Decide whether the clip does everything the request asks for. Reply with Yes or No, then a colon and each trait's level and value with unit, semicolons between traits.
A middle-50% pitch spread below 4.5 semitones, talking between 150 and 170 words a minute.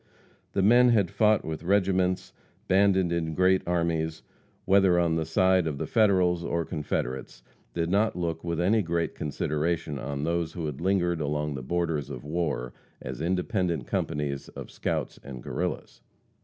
Yes: average, 3.6 semitones; average, 160 wpm